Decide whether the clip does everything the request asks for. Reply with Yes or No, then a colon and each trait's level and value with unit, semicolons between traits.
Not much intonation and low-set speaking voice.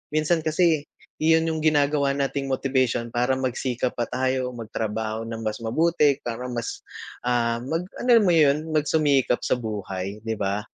No: average, 4.8 semitones; low, 130 Hz